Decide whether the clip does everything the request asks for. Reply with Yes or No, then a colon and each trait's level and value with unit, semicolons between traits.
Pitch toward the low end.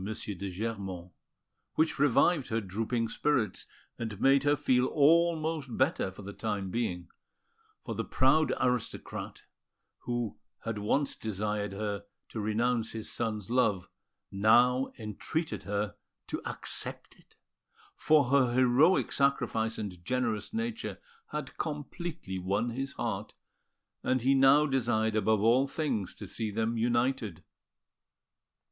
Yes: low, 115 Hz